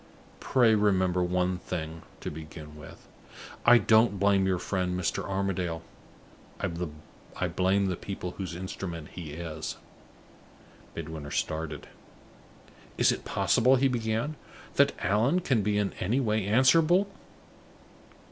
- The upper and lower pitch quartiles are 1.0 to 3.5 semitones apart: No, average, 4.6 semitones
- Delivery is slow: Yes, slow, 120 wpm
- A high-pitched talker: No, very low, 95 Hz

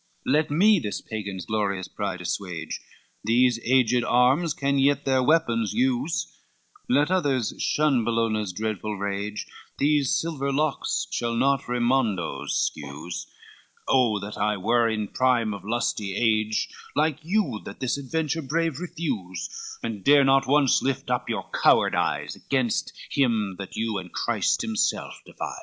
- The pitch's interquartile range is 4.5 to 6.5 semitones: Yes, average, 4.8 semitones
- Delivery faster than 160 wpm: No, average, 145 wpm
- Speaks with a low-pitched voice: Yes, low, 120 Hz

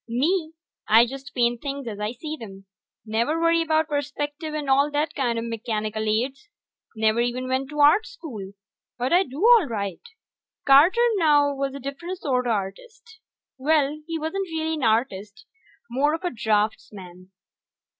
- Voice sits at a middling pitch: No, very high, 275 Hz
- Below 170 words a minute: Yes, average, 155 wpm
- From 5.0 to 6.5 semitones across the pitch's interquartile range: Yes, wide, 5.6 semitones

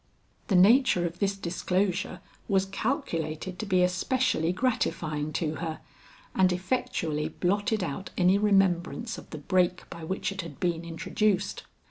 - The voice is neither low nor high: Yes, medium, 180 Hz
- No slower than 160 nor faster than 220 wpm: No, average, 140 wpm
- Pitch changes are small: No, average, 3.1 semitones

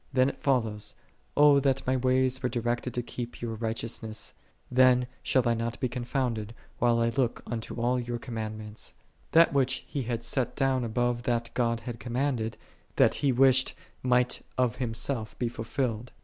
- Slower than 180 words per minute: Yes, average, 165 wpm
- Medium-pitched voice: No, low, 120 Hz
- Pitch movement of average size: No, narrow, 1.9 semitones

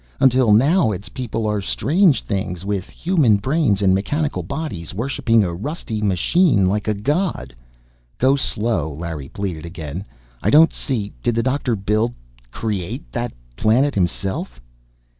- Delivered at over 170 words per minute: No, average, 145 wpm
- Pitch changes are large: Yes, wide, 6.0 semitones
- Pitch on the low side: Yes, low, 105 Hz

